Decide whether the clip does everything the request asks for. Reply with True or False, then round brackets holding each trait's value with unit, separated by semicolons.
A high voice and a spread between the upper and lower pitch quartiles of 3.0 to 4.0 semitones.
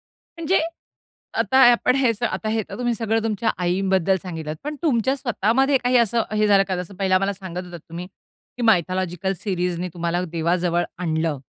False (195 Hz; 4.7 semitones)